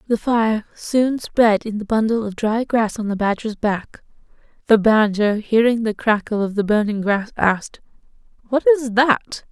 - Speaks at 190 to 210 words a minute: No, average, 170 wpm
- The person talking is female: Yes, female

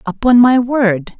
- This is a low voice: No, high, 230 Hz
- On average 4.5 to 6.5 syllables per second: No, 3.9 syllables/s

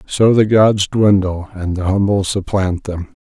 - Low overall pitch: Yes, low, 100 Hz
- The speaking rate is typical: Yes, average, 165 wpm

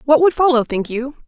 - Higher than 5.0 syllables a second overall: Yes, 5.7 syllables/s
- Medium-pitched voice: No, very high, 270 Hz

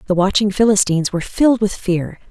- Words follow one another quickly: No, average, 180 wpm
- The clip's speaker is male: No, female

